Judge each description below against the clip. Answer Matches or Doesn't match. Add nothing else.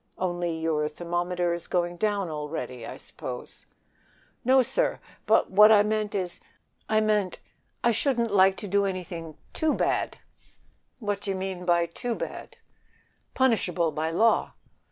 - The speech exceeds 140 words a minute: Doesn't match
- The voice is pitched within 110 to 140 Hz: Doesn't match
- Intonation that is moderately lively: Matches